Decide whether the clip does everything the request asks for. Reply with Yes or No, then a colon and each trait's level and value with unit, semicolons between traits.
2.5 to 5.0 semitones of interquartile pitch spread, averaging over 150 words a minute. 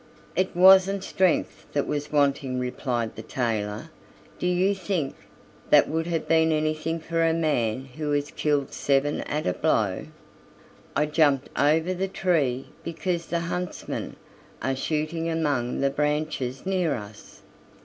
No: average, 3.7 semitones; average, 140 wpm